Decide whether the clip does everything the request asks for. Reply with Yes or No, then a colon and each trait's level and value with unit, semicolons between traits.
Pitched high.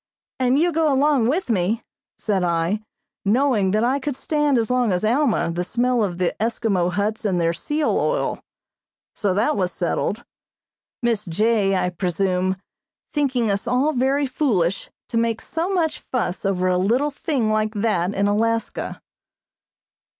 Yes: high, 220 Hz